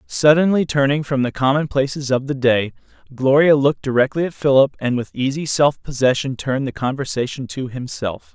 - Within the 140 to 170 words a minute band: Yes, average, 165 wpm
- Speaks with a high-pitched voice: No, low, 135 Hz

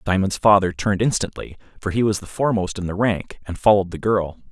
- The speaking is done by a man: Yes, male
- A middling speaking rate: No, fast, 215 wpm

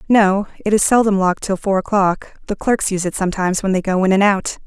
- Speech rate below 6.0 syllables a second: No, 6.3 syllables/s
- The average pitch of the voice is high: Yes, high, 195 Hz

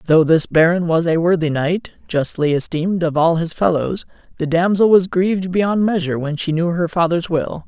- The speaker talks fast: No, average, 195 wpm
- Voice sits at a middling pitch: Yes, medium, 170 Hz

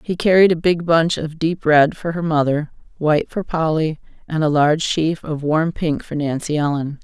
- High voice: No, medium, 160 Hz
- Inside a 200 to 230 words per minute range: Yes, fast, 205 wpm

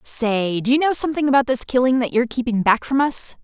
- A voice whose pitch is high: Yes, very high, 250 Hz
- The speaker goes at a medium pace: No, fast, 245 wpm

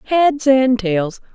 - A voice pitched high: Yes, high, 245 Hz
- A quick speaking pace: No, slow, 135 wpm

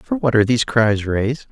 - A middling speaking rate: No, fast, 235 wpm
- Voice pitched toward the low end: Yes, low, 120 Hz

